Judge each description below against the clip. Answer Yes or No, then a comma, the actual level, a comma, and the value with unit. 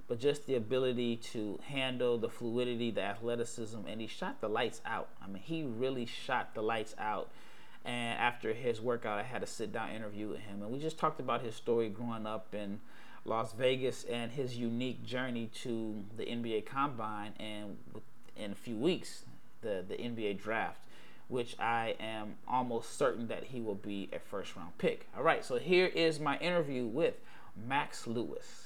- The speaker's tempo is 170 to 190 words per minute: Yes, average, 185 wpm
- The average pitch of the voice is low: Yes, low, 115 Hz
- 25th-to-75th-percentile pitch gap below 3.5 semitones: Yes, average, 2.9 semitones